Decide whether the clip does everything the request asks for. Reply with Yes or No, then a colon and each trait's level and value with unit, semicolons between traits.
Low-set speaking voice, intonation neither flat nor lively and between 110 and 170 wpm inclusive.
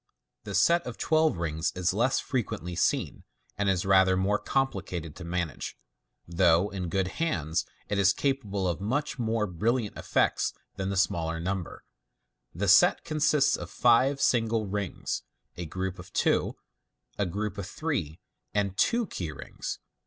Yes: low, 100 Hz; average, 4.8 semitones; average, 155 wpm